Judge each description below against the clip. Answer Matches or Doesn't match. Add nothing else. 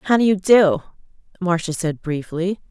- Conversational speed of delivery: Matches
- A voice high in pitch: Doesn't match